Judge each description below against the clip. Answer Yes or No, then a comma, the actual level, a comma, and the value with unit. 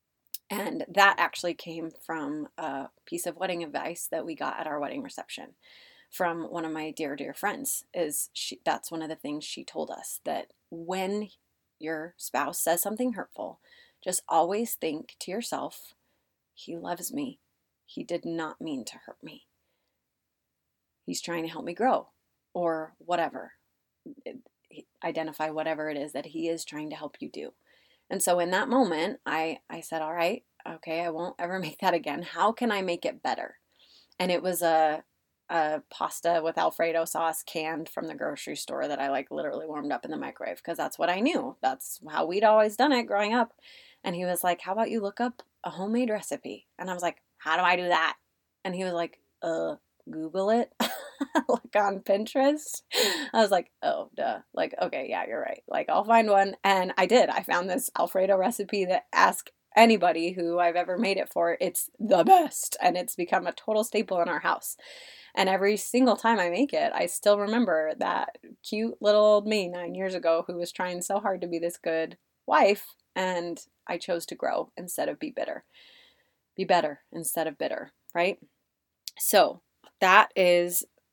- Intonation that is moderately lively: Yes, average, 4.1 semitones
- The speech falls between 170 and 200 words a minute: Yes, average, 190 wpm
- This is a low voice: No, medium, 180 Hz